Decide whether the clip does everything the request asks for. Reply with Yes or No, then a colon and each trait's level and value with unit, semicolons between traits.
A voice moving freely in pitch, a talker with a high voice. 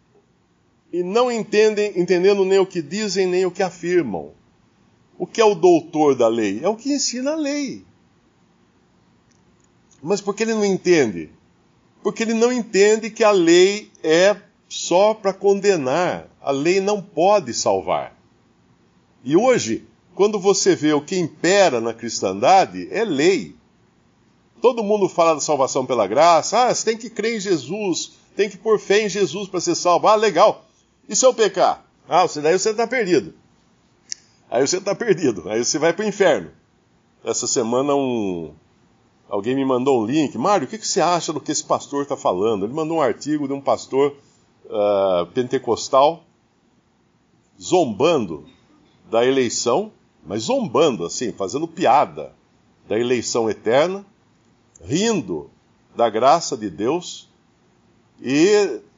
Yes: wide, 5.8 semitones; high, 195 Hz